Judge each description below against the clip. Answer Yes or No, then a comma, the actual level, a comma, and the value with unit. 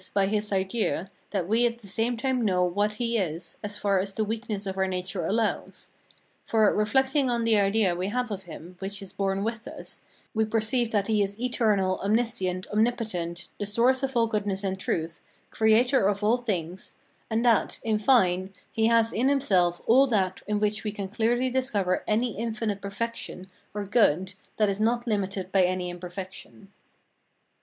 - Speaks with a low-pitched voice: No, high, 210 Hz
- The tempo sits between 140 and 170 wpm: No, average, 180 wpm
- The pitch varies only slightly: No, average, 3.3 semitones